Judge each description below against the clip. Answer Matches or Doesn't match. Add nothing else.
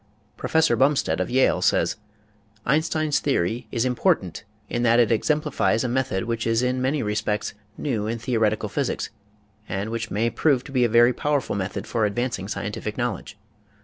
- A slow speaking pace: Doesn't match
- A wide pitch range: Doesn't match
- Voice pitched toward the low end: Matches